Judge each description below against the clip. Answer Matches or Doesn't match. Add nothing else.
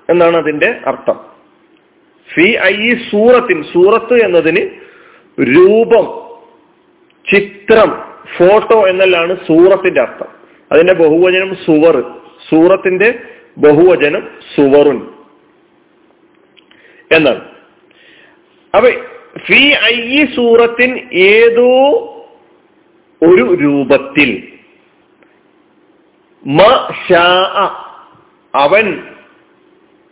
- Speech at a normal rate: Doesn't match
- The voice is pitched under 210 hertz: Doesn't match